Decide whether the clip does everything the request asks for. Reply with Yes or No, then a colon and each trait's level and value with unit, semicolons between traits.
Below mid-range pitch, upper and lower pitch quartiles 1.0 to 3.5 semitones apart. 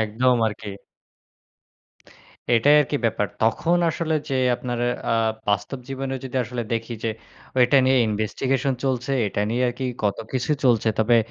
Yes: low, 125 Hz; average, 3.2 semitones